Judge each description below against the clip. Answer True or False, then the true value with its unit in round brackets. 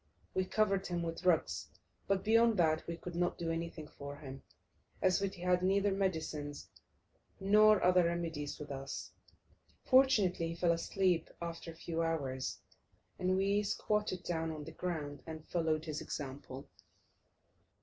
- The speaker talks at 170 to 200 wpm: False (150 wpm)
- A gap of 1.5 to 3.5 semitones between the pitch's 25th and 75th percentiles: True (3.2 semitones)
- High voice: False (170 Hz)